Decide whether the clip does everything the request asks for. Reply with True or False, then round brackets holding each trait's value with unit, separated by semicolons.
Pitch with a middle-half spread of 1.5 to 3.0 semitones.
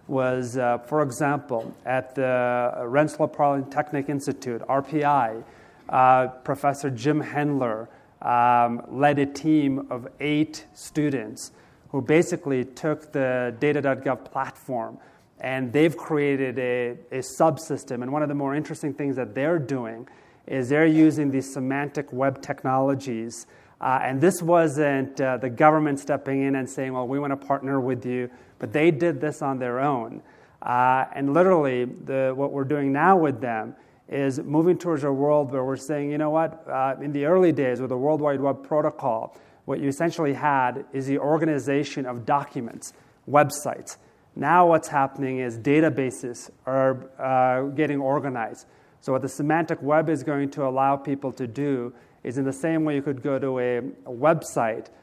True (2.5 semitones)